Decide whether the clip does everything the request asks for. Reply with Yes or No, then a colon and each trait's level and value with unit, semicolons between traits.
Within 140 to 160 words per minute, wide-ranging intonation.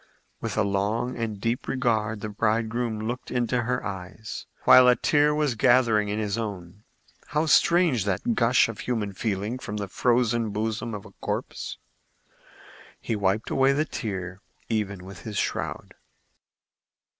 No: average, 150 wpm; average, 3.1 semitones